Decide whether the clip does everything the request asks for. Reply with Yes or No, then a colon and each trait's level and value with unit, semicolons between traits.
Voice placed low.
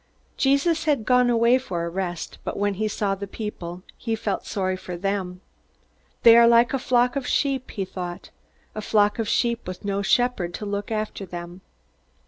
No: high, 210 Hz